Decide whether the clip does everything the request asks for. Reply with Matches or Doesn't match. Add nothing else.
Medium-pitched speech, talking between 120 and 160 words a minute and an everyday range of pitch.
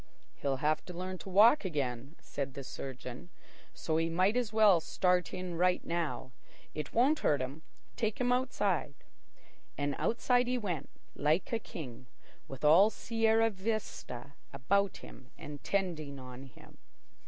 Doesn't match